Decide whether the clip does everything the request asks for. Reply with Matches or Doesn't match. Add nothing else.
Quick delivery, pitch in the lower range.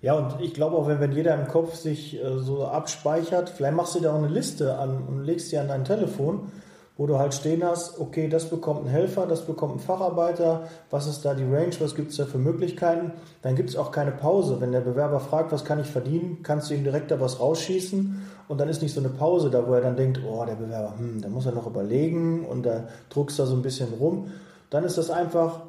Doesn't match